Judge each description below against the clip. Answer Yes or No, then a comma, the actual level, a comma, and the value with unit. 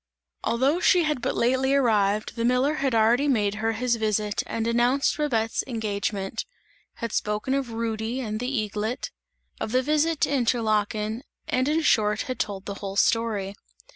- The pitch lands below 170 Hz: No, high, 230 Hz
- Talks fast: No, average, 165 wpm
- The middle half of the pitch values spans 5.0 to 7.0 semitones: No, average, 3.5 semitones